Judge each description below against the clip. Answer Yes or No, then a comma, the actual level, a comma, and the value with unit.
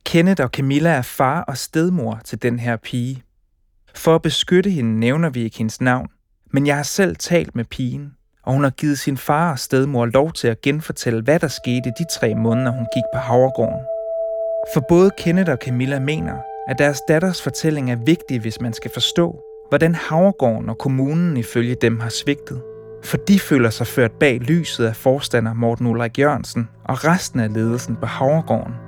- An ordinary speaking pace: Yes, average, 190 wpm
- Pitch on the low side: Yes, low, 130 Hz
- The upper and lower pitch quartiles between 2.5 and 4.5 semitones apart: No, average, 5.3 semitones